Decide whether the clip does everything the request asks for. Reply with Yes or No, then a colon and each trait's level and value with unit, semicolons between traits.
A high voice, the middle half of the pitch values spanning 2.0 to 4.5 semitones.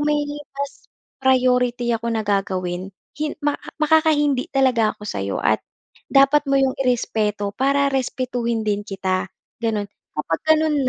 No: very high, 250 Hz; average, 5.0 semitones